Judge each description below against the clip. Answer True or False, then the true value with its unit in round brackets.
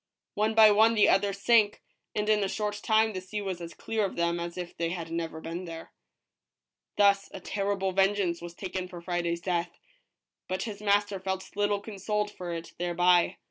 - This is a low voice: False (190 Hz)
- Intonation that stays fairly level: False (3.1 semitones)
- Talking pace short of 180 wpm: False (190 wpm)